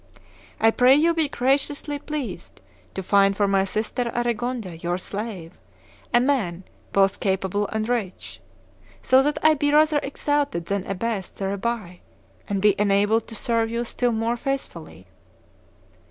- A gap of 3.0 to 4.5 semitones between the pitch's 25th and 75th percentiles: No, average, 5.1 semitones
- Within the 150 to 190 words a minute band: No, average, 140 wpm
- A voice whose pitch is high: Yes, high, 225 Hz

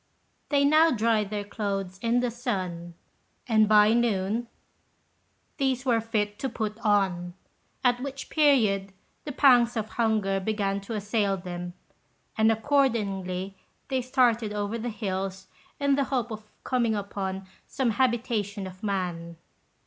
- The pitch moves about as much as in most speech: Yes, average, 3.7 semitones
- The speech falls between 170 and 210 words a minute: No, slow, 135 wpm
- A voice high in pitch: Yes, high, 215 Hz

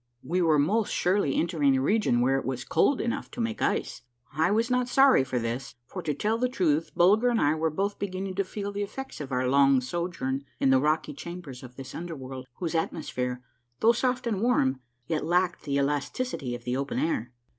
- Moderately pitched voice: Yes, medium, 160 Hz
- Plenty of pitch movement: Yes, wide, 7.1 semitones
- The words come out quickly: Yes, fast, 210 wpm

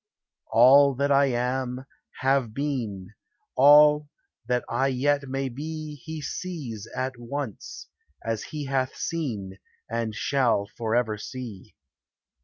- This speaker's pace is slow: Yes, slow, 115 wpm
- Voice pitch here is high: No, low, 130 Hz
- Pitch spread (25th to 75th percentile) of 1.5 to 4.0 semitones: Yes, average, 3.4 semitones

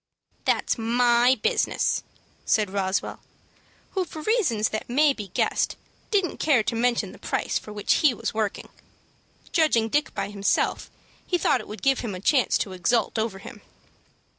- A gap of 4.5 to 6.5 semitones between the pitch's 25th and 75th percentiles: Yes, average, 5.1 semitones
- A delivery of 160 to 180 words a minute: Yes, average, 165 wpm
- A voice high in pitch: Yes, high, 235 Hz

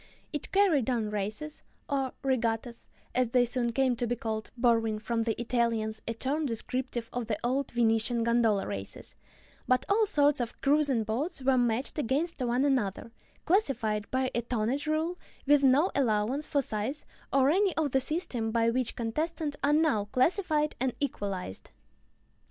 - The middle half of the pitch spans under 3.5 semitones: No, average, 4.1 semitones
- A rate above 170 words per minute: No, average, 160 wpm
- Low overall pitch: No, very high, 250 Hz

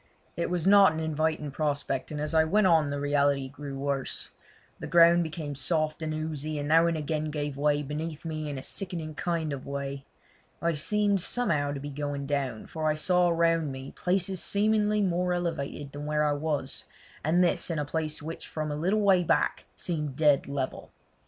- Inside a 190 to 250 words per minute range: Yes, average, 195 wpm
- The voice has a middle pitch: Yes, medium, 155 Hz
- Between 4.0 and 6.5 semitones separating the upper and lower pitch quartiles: No, average, 2.8 semitones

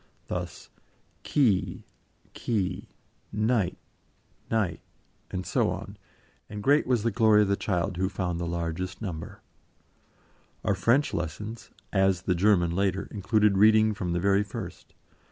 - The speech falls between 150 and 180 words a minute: No, slow, 135 wpm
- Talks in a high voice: No, low, 100 Hz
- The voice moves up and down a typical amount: Yes, average, 3.1 semitones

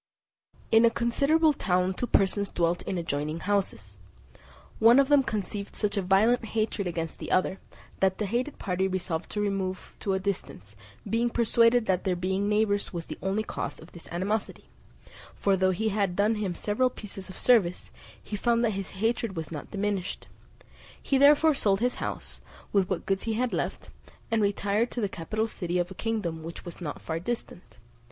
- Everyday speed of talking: Yes, average, 185 wpm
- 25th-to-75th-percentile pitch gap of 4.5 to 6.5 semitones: No, average, 3.7 semitones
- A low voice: No, high, 200 Hz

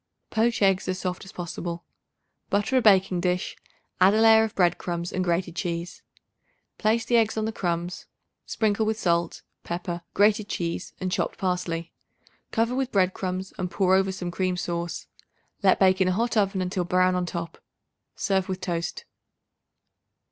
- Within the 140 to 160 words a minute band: No, average, 170 wpm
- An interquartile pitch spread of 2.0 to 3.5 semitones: Yes, average, 2.9 semitones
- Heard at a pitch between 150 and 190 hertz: Yes, medium, 185 Hz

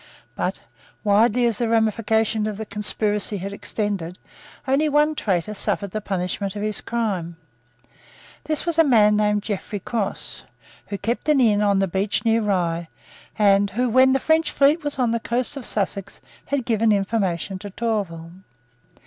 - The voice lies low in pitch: No, high, 210 Hz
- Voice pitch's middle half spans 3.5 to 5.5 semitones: No, average, 3.1 semitones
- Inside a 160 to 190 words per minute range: Yes, average, 165 wpm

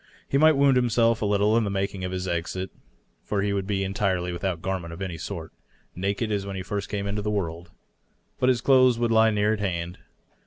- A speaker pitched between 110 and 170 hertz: No, low, 100 Hz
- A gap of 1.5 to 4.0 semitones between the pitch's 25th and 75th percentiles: Yes, average, 3.1 semitones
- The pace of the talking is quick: Yes, fast, 220 wpm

